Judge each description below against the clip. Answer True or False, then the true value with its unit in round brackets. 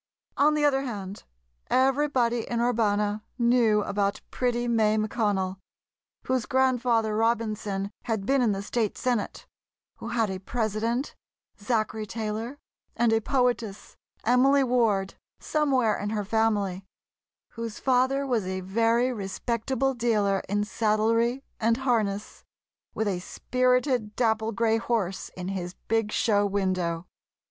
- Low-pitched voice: False (225 Hz)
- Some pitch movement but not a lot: True (3.1 semitones)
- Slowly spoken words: True (125 wpm)